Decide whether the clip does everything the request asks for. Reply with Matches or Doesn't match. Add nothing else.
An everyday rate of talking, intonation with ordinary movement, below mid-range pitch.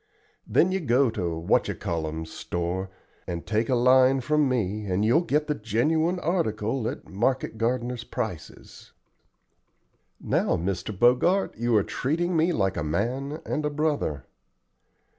Doesn't match